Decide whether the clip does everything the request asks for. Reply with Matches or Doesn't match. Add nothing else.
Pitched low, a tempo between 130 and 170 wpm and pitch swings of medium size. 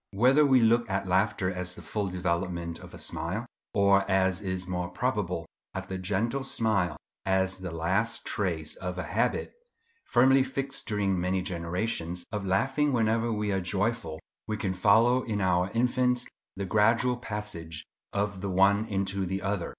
Matches